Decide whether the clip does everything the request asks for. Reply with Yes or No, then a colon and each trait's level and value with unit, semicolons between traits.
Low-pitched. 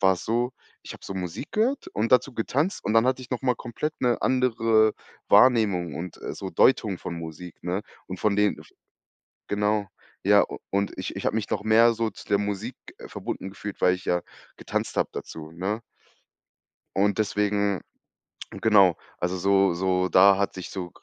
Yes: low, 100 Hz